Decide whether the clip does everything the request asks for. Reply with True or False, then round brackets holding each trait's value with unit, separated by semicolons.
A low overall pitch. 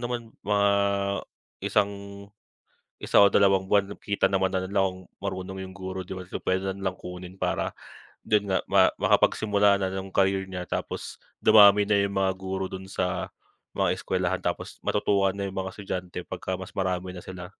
True (95 Hz)